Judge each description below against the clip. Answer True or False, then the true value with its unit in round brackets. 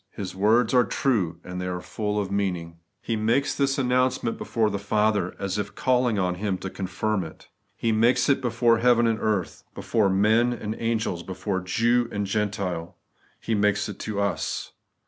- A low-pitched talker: True (105 Hz)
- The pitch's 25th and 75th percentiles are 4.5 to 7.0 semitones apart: False (3.3 semitones)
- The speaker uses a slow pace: False (180 wpm)